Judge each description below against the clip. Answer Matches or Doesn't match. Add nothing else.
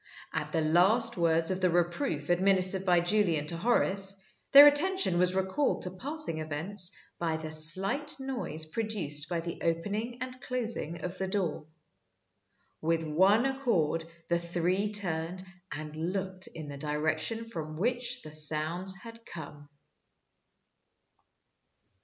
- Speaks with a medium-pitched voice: Matches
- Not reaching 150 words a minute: Matches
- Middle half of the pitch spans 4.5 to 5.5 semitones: Matches